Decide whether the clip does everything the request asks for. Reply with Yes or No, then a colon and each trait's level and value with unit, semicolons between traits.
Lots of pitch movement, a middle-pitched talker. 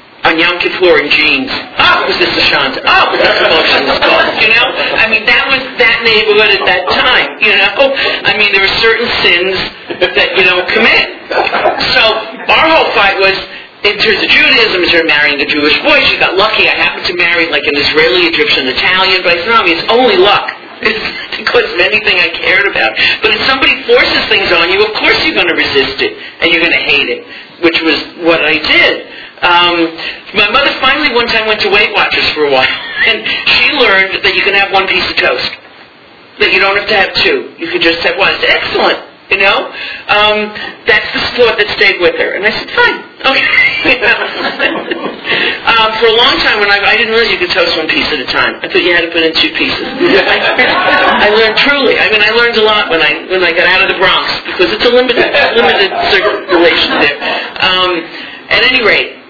No: wide, 7.2 semitones; high, 210 Hz